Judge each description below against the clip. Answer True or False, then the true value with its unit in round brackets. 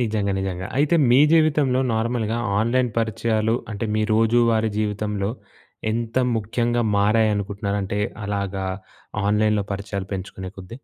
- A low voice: True (110 Hz)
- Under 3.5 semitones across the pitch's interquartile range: True (2.5 semitones)